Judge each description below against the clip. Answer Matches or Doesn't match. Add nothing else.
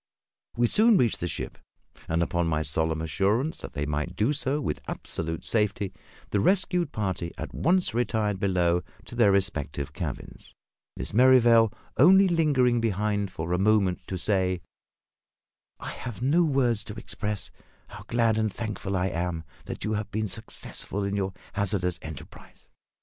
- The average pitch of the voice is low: Matches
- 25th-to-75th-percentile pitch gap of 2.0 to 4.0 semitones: Doesn't match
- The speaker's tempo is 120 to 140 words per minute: Doesn't match